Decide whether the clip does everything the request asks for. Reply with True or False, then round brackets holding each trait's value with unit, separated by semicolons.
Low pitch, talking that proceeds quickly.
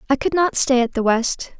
False (265 Hz; 265 wpm)